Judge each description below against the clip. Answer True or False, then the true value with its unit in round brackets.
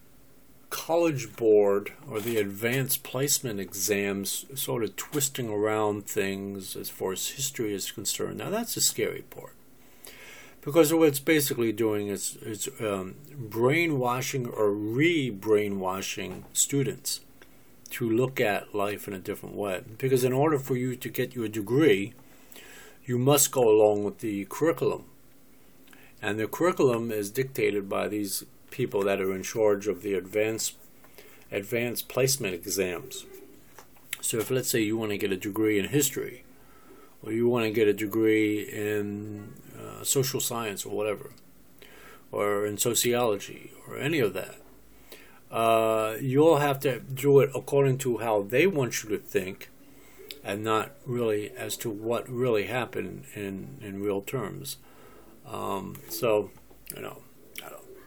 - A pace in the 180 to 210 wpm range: False (145 wpm)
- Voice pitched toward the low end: True (110 Hz)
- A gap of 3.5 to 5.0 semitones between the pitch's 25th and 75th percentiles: True (4.4 semitones)